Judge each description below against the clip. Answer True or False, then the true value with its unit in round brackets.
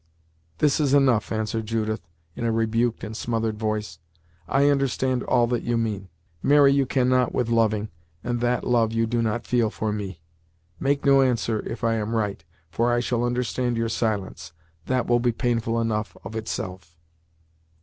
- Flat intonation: True (2.1 semitones)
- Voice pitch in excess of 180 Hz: False (115 Hz)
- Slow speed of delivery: False (170 wpm)